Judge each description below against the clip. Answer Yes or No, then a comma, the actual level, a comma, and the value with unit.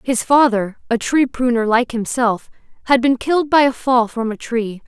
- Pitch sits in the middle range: No, high, 245 Hz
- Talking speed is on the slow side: No, average, 195 wpm